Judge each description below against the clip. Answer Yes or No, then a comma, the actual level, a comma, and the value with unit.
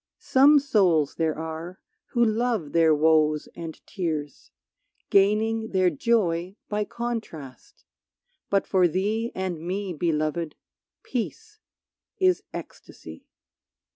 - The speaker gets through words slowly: Yes, slow, 105 wpm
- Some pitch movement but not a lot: No, wide, 5.7 semitones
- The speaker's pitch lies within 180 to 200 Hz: Yes, medium, 185 Hz